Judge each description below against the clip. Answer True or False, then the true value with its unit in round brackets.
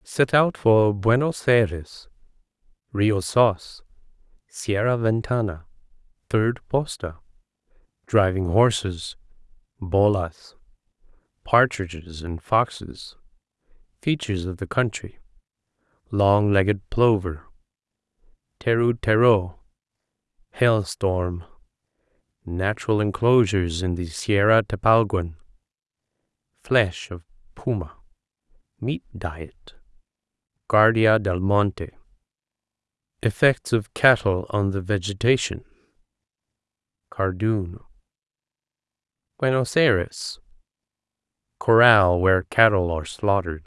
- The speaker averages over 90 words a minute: False (50 wpm)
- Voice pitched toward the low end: True (100 Hz)